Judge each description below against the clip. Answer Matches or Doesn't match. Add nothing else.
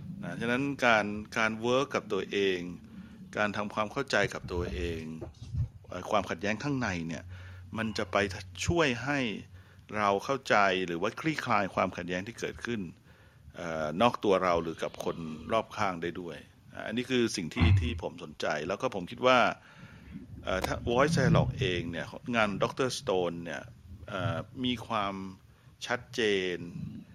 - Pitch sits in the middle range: Doesn't match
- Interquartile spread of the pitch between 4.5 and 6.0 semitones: Matches